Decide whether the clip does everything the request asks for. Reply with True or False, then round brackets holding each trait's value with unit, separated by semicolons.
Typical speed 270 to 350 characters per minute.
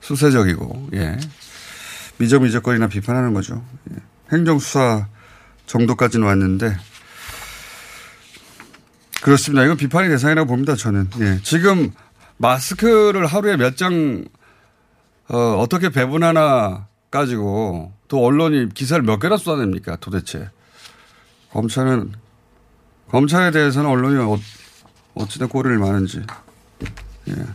False (250 characters per minute)